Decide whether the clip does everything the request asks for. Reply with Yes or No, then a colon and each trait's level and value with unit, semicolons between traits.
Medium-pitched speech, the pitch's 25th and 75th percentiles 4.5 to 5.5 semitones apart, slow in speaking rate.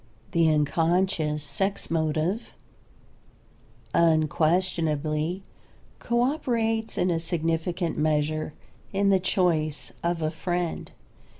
No: medium, 165 Hz; average, 3.2 semitones; slow, 90 wpm